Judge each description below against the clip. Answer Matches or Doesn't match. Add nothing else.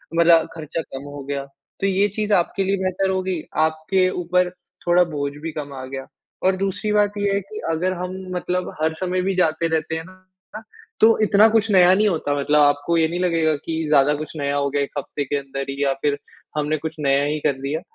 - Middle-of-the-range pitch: Matches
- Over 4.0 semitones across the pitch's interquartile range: Matches